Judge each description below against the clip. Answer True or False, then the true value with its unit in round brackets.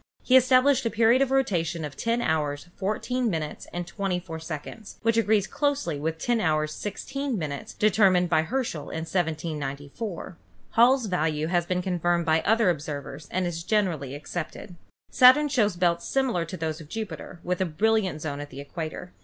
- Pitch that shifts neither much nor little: False (5.9 semitones)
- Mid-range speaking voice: True (175 Hz)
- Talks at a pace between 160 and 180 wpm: True (170 wpm)